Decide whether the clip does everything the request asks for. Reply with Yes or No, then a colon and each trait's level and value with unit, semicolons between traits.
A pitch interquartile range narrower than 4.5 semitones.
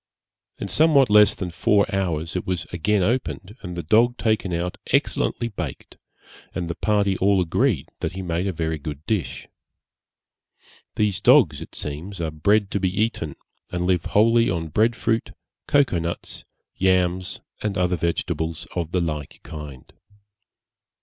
Yes: average, 4.0 semitones